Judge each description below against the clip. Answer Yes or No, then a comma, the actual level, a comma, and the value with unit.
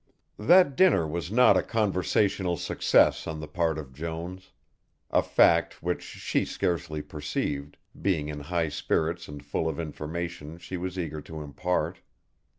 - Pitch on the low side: Yes, very low, 85 Hz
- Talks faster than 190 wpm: No, average, 150 wpm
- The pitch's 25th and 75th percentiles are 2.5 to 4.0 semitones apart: Yes, average, 3.1 semitones